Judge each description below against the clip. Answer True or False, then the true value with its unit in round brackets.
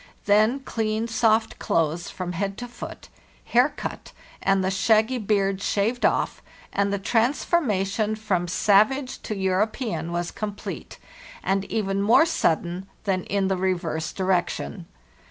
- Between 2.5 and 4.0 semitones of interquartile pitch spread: True (2.9 semitones)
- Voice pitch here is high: True (200 Hz)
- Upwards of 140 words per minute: False (135 wpm)